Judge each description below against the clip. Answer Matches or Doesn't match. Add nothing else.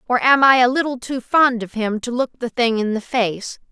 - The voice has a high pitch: Matches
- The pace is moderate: Doesn't match